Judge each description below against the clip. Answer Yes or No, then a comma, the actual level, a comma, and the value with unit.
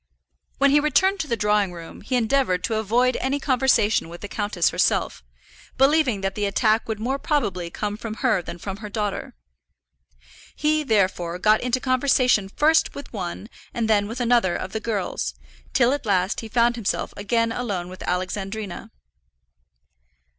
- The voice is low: No, high, 220 Hz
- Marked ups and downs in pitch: No, average, 4.5 semitones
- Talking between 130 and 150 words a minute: No, average, 165 wpm